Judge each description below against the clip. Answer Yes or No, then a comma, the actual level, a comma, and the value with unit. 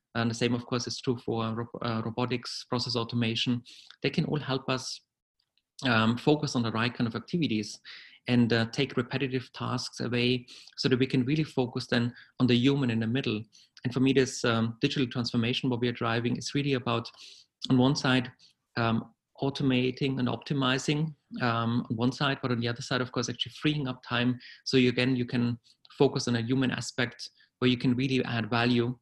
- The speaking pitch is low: Yes, low, 125 Hz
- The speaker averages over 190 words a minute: Yes, average, 200 wpm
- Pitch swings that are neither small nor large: No, narrow, 1.7 semitones